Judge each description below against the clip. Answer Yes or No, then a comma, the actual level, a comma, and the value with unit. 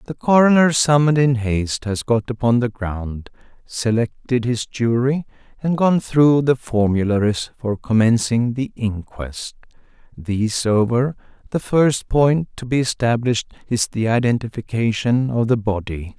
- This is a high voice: No, low, 120 Hz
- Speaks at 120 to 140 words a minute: Yes, slow, 135 wpm